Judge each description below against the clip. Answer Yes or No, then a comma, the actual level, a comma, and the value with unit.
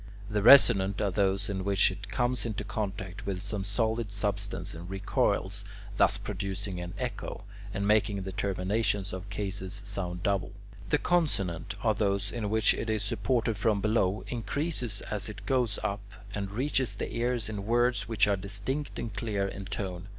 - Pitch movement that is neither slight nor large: No, narrow, 2.3 semitones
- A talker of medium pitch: No, low, 100 Hz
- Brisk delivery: No, average, 170 wpm